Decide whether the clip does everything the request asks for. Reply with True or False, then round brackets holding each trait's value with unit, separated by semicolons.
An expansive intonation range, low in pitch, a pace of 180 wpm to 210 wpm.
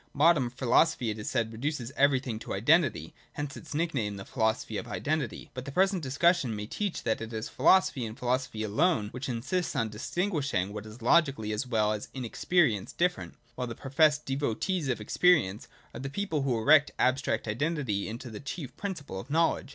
True (5.7 semitones; 130 Hz; 185 wpm)